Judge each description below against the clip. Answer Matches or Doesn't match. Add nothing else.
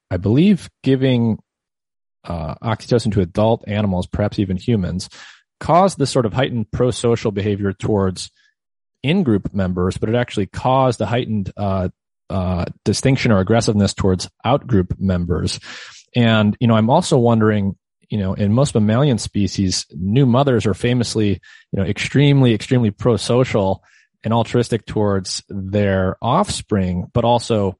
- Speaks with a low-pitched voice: Matches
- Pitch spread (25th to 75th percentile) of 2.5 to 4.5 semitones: Matches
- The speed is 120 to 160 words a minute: Matches